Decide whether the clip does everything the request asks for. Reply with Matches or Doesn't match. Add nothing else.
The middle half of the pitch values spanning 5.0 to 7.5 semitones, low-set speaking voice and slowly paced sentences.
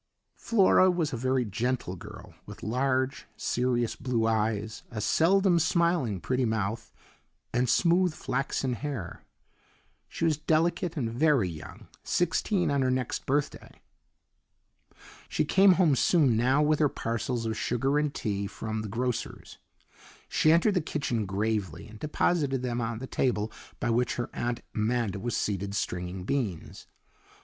Doesn't match